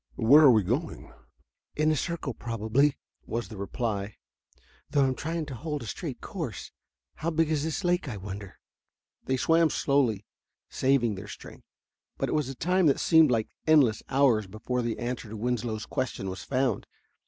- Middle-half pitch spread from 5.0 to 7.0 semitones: Yes, wide, 5.5 semitones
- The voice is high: No, low, 130 Hz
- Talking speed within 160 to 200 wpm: Yes, average, 175 wpm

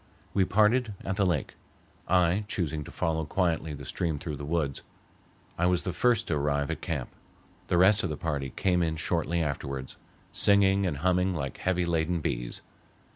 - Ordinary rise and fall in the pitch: Yes, average, 3.8 semitones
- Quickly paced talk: No, average, 180 wpm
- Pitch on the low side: Yes, very low, 85 Hz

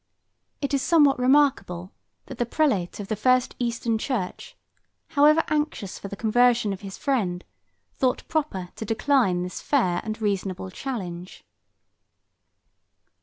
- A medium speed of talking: No, slow, 130 wpm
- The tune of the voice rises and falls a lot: Yes, wide, 6.2 semitones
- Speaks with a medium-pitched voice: No, high, 230 Hz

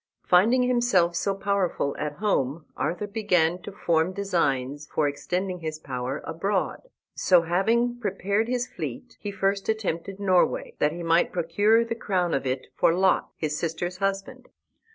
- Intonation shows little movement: No, average, 3.9 semitones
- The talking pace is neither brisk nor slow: Yes, average, 155 wpm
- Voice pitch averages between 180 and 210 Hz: Yes, medium, 185 Hz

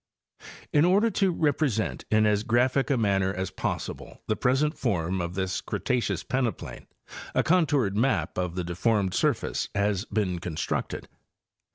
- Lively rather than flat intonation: Yes, wide, 6.1 semitones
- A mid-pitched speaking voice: No, low, 110 Hz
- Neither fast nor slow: Yes, average, 145 wpm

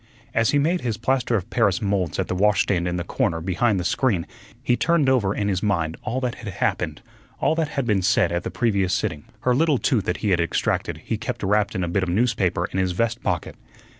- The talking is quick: Yes, fast, 235 wpm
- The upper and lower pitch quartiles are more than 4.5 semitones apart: Yes, average, 5.3 semitones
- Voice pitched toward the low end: Yes, low, 100 Hz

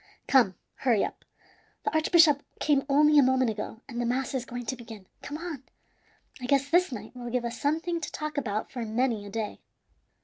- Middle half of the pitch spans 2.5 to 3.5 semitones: No, average, 3.9 semitones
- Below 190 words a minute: No, average, 200 wpm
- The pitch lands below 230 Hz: No, very high, 260 Hz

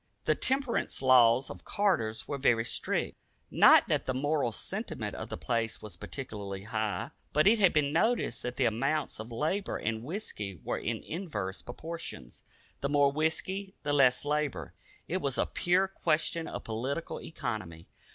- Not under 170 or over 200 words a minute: No, average, 160 wpm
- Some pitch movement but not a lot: No, wide, 6.3 semitones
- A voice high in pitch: No, medium, 140 Hz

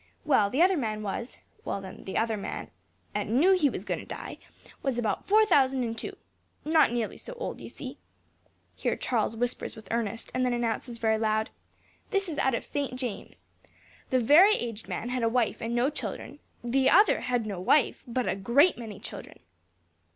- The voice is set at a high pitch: Yes, high, 240 Hz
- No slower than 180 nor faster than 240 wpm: Yes, average, 195 wpm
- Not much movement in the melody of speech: No, average, 3.9 semitones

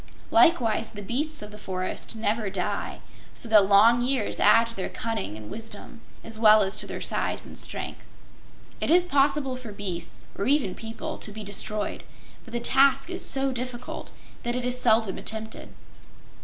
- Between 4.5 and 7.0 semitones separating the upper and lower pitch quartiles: No, average, 3.6 semitones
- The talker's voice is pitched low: No, high, 225 Hz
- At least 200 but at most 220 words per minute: No, average, 175 wpm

